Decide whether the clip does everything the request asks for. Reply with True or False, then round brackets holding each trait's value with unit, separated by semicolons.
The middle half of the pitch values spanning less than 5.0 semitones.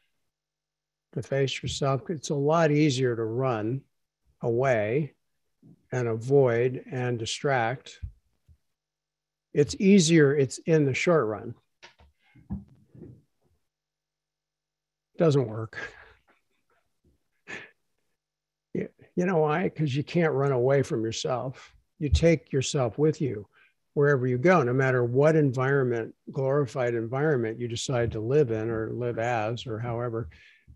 True (4.5 semitones)